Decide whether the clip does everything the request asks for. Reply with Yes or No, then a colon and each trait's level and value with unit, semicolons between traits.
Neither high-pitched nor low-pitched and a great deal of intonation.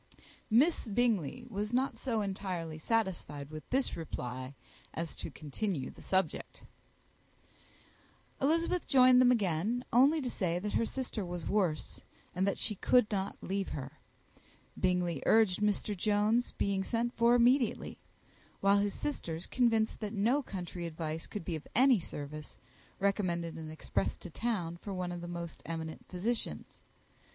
No: high, 195 Hz; wide, 5.7 semitones